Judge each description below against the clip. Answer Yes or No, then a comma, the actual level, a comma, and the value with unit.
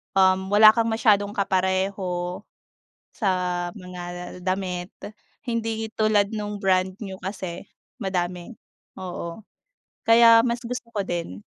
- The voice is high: Yes, high, 195 Hz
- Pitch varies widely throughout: No, average, 3.2 semitones